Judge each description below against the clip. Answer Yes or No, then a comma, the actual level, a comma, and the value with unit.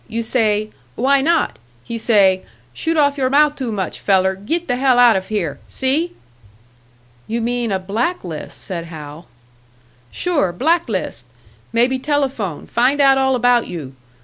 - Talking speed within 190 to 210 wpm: No, average, 155 wpm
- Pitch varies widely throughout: Yes, wide, 6.2 semitones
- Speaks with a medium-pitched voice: No, high, 235 Hz